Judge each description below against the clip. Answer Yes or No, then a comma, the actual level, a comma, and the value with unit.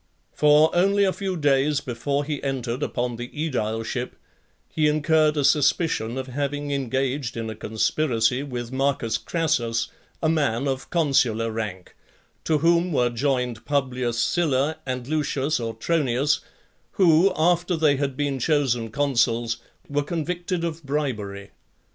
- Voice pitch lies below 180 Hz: Yes, medium, 140 Hz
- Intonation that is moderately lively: Yes, average, 4.2 semitones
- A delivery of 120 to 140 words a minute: Yes, slow, 135 wpm